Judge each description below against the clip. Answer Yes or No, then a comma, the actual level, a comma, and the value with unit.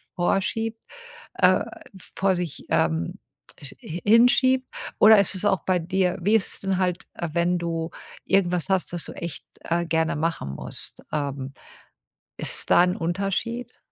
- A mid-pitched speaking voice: Yes, medium, 180 Hz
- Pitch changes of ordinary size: Yes, average, 3.0 semitones